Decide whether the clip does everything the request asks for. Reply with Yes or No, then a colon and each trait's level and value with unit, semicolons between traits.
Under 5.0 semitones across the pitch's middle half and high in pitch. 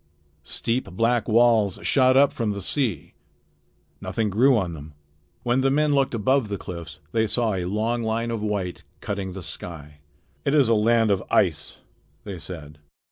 No: average, 4.6 semitones; low, 110 Hz